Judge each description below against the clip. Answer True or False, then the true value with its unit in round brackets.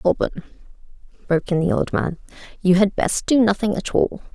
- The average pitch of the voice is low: False (195 Hz)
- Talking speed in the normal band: True (180 wpm)